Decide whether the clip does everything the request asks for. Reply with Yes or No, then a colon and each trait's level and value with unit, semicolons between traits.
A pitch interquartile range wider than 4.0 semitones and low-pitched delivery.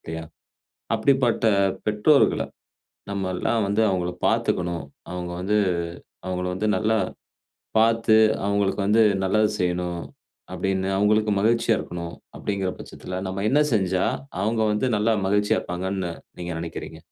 No: average, 3.1 semitones; low, 100 Hz